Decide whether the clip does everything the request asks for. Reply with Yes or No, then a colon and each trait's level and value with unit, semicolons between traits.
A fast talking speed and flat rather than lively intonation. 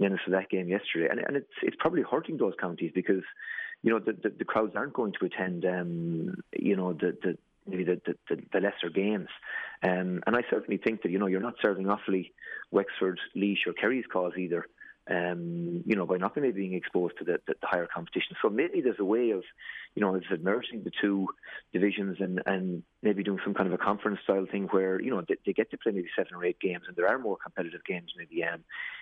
Yes: fast, 235 wpm; narrow, 1.9 semitones